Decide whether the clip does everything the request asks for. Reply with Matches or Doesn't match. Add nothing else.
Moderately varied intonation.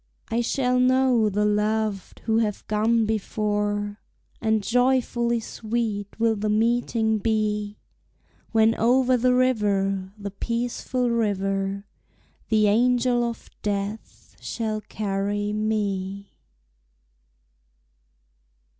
Doesn't match